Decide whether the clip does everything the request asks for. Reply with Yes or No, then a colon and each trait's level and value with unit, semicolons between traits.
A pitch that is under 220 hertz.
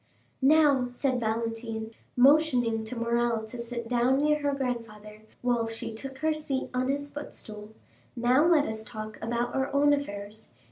No: high, 245 Hz